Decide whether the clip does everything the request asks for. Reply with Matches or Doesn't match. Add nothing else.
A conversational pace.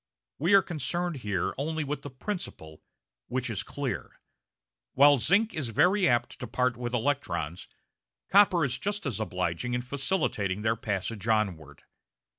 Matches